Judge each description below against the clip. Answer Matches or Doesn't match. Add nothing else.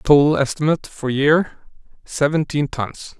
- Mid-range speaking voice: Matches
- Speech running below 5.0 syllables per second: Matches